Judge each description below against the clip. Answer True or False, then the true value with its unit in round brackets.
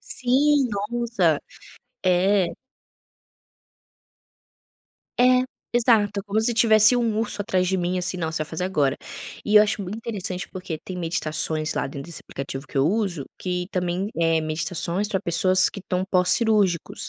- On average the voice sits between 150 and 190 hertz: True (185 Hz)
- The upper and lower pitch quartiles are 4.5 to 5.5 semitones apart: False (3.9 semitones)